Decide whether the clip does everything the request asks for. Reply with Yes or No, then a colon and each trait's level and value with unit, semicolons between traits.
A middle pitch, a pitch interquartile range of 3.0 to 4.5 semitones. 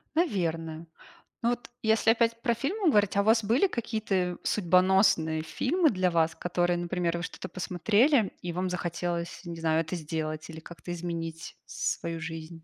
No: medium, 180 Hz; average, 4.9 semitones